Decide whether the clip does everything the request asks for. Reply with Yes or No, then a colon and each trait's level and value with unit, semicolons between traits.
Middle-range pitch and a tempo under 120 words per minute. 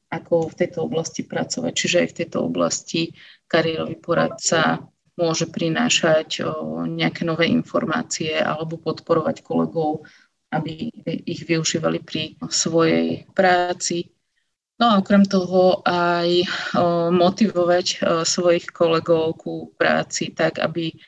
Yes: medium, 165 Hz; slow, 110 wpm